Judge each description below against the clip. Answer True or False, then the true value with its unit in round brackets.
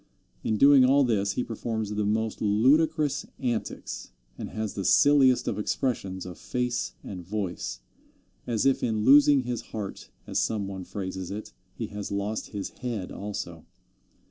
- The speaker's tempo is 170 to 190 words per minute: False (155 wpm)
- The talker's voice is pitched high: False (110 Hz)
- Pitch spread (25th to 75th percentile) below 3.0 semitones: False (4.0 semitones)